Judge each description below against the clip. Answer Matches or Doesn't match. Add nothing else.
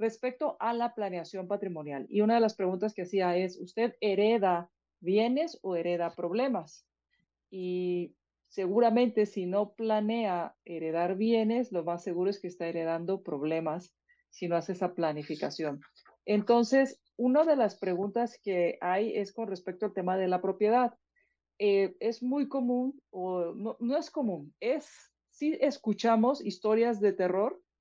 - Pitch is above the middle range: Matches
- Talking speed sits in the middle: Matches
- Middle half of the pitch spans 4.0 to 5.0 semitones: Matches